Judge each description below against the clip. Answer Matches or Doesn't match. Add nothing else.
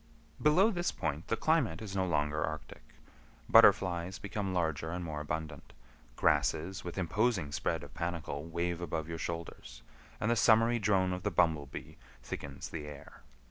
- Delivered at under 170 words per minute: Matches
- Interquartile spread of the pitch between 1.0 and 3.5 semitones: Doesn't match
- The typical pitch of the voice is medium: Doesn't match